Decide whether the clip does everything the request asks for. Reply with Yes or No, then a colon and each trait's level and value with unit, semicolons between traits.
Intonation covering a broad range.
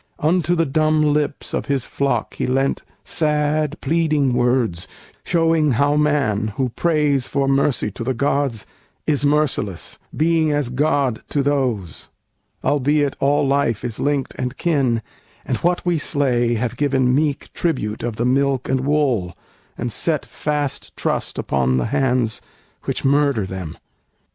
No: average, 3.6 semitones